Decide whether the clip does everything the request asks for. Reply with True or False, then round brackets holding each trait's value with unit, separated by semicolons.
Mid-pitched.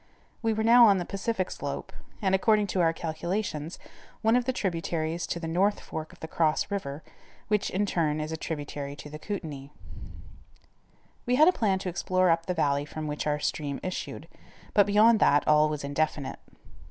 True (170 Hz)